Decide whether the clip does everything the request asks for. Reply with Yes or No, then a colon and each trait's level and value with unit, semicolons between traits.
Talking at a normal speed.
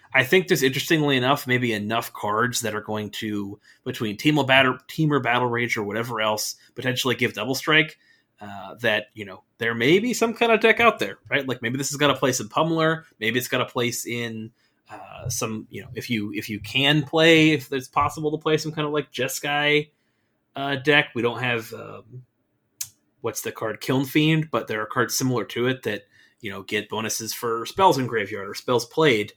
No: fast, 215 wpm